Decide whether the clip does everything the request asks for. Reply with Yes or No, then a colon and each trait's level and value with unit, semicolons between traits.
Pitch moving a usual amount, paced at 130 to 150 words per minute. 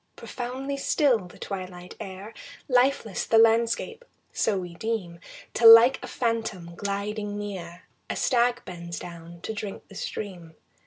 Yes: average, 4.4 semitones; average, 140 wpm